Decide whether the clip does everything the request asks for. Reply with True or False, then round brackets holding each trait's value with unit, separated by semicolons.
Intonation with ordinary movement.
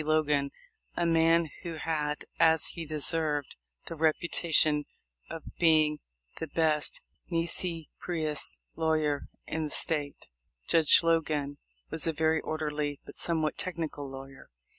False (1.7 semitones)